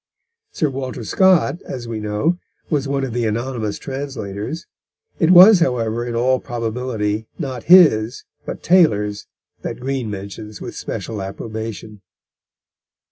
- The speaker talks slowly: Yes, slow, 130 wpm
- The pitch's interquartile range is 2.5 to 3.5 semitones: No, average, 4.3 semitones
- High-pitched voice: No, low, 120 Hz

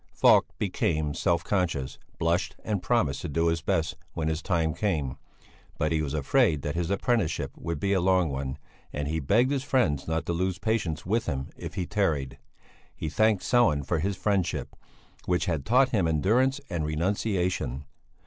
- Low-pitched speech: Yes, very low, 85 Hz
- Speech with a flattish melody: No, average, 4.6 semitones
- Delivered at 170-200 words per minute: Yes, average, 175 wpm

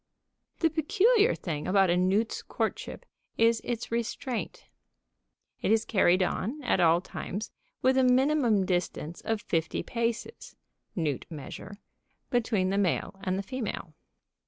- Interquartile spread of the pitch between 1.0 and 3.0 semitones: No, average, 5.1 semitones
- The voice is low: No, high, 210 Hz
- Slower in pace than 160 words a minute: Yes, slow, 135 wpm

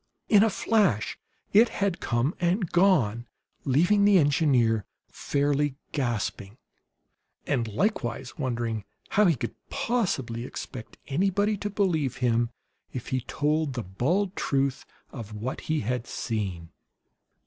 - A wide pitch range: Yes, wide, 7.6 semitones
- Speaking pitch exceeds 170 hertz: No, low, 135 Hz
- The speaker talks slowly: Yes, slow, 125 wpm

